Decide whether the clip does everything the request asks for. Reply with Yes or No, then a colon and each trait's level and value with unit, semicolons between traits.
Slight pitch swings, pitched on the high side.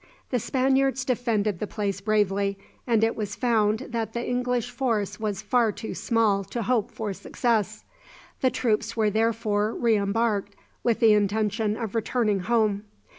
Yes: narrow, 2.3 semitones; high, 220 Hz